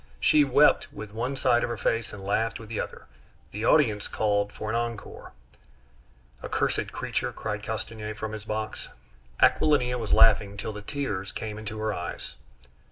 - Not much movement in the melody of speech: Yes, narrow, 2.2 semitones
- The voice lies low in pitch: Yes, low, 110 Hz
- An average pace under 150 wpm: No, average, 165 wpm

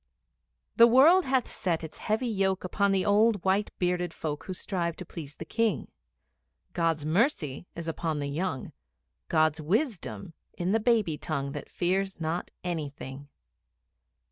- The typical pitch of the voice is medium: Yes, medium, 180 Hz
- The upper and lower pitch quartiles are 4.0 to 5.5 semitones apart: Yes, average, 4.7 semitones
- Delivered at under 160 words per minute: Yes, average, 145 wpm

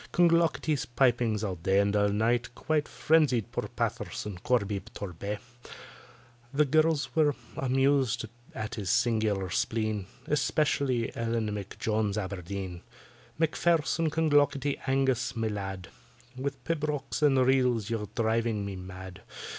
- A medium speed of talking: No, slow, 120 wpm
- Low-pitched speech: Yes, low, 115 Hz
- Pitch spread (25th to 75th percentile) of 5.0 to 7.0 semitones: Yes, wide, 5.6 semitones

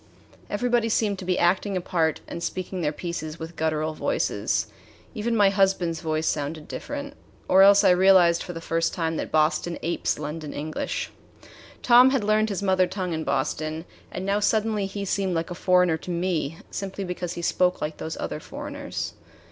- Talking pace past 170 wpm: Yes, average, 180 wpm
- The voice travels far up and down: No, average, 3.5 semitones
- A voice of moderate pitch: Yes, medium, 180 Hz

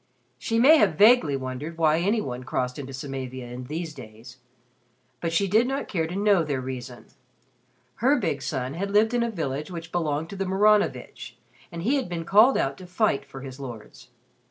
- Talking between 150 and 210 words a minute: Yes, average, 195 wpm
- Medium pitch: Yes, medium, 160 Hz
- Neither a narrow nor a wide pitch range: No, wide, 7.3 semitones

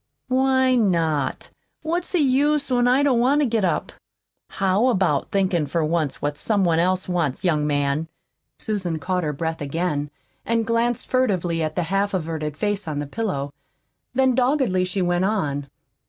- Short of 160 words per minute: No, average, 165 wpm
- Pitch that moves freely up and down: Yes, wide, 7.3 semitones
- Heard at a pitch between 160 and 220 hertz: Yes, medium, 185 Hz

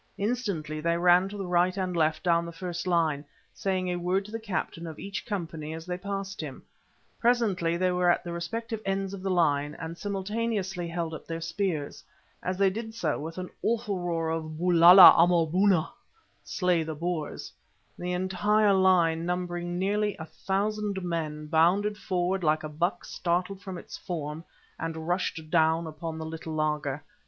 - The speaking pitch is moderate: Yes, medium, 175 Hz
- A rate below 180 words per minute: Yes, average, 170 wpm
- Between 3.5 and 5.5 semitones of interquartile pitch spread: No, average, 3.0 semitones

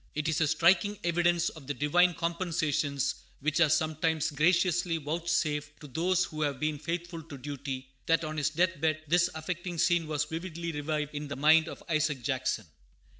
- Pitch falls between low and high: Yes, medium, 155 Hz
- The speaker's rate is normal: Yes, average, 175 wpm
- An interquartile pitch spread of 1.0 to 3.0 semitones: Yes, narrow, 2.5 semitones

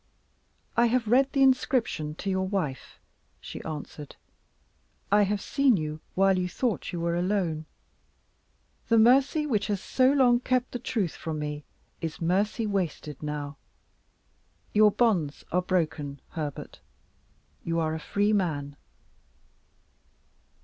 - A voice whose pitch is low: No, high, 190 Hz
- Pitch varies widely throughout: Yes, wide, 6.7 semitones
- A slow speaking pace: Yes, slow, 130 wpm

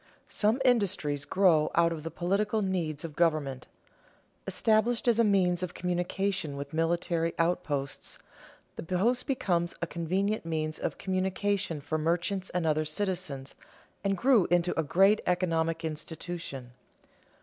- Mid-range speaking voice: Yes, medium, 175 Hz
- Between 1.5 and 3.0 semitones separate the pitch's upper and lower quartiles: No, average, 3.6 semitones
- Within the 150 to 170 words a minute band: No, average, 140 wpm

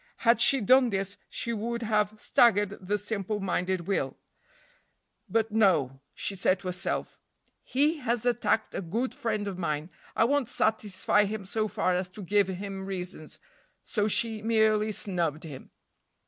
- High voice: Yes, high, 205 Hz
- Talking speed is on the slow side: No, average, 155 wpm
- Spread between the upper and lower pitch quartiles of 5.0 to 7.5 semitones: No, average, 3.2 semitones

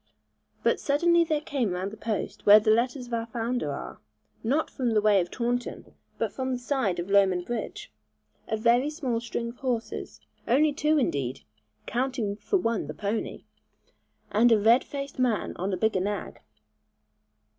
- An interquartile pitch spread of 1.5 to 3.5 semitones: No, average, 4.0 semitones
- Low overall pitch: No, high, 230 Hz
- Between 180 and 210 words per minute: No, average, 170 wpm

